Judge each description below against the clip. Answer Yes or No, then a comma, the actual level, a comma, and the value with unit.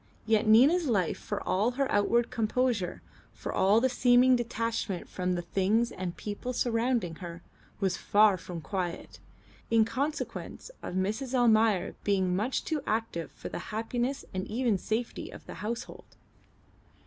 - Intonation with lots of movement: No, average, 4.4 semitones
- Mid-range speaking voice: No, high, 220 Hz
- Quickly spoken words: No, average, 150 wpm